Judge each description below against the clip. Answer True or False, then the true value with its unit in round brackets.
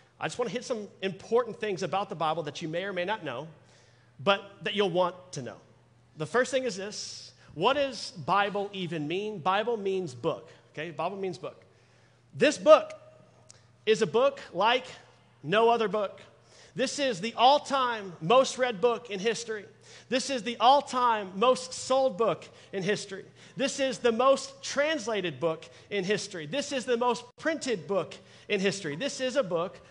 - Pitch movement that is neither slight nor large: False (6.5 semitones)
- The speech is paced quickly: False (180 wpm)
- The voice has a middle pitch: False (210 Hz)